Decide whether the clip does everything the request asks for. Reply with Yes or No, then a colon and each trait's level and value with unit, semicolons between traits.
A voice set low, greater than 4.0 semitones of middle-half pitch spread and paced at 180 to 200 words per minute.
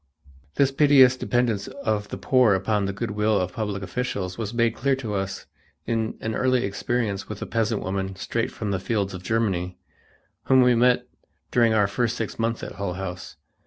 No: low, 110 Hz; average, 3.7 semitones; average, 190 wpm